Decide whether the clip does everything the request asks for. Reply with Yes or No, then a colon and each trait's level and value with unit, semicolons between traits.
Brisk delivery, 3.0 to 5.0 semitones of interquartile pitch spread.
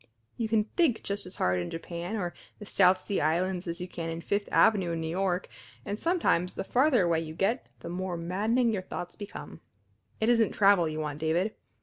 Yes: fast, 210 wpm; average, 3.9 semitones